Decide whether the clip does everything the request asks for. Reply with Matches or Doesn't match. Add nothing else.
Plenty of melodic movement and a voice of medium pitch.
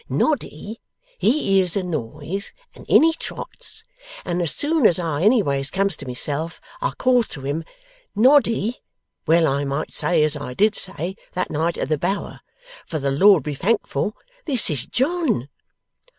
Matches